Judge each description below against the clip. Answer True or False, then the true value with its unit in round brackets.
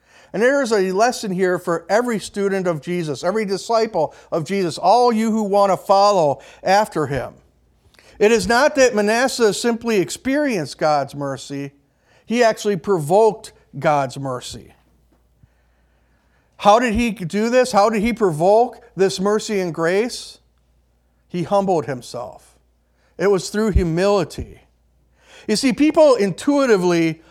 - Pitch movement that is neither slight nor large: False (7.0 semitones)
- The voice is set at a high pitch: True (195 Hz)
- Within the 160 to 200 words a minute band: False (135 wpm)